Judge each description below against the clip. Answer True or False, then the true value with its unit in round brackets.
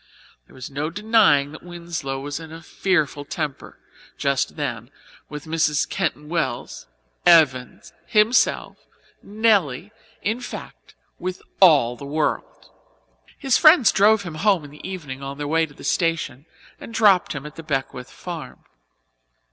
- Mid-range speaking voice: True (160 Hz)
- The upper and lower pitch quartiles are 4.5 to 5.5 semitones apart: True (5.1 semitones)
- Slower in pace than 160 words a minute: True (145 wpm)